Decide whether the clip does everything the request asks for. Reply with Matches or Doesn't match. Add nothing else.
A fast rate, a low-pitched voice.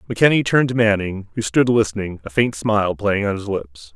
Matches